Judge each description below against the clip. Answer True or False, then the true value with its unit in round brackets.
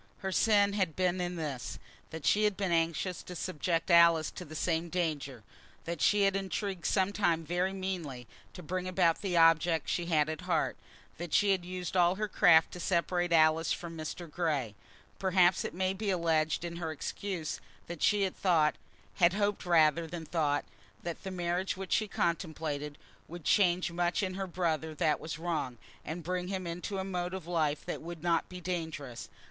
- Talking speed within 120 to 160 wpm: False (190 wpm)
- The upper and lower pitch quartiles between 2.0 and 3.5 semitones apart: True (2.5 semitones)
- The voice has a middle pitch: True (175 Hz)